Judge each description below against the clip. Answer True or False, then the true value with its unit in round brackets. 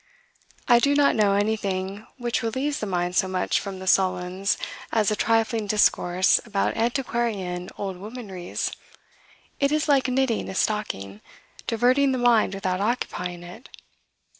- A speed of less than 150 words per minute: True (140 wpm)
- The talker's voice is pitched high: True (210 Hz)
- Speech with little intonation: False (4.3 semitones)